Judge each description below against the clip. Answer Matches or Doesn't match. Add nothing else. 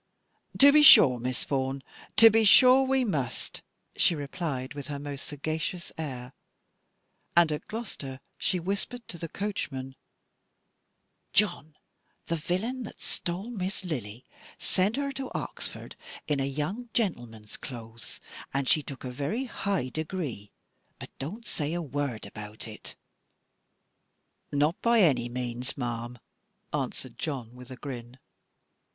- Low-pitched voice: Doesn't match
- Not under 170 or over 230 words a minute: Doesn't match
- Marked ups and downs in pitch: Matches